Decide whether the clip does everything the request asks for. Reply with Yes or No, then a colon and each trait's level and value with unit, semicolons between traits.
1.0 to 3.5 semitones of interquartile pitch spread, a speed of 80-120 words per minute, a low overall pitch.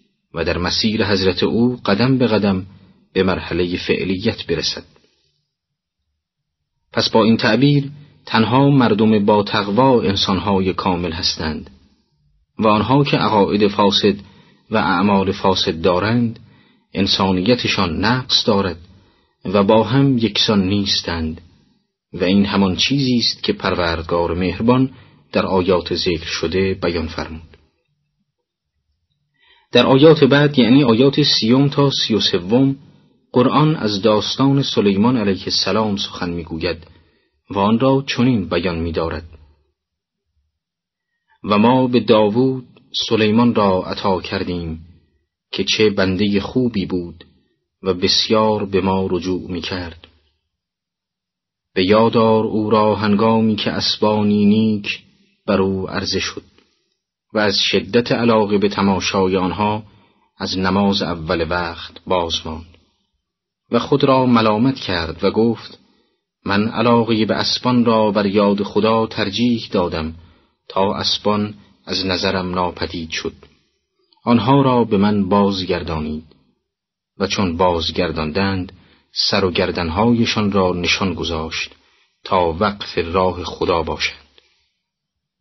No: average, 4.4 semitones; average, 115 wpm; low, 100 Hz